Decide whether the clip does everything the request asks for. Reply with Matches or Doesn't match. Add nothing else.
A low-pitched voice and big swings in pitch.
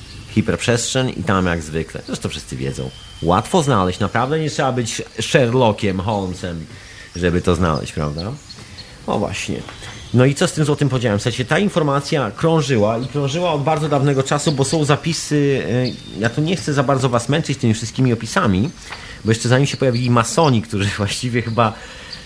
Matches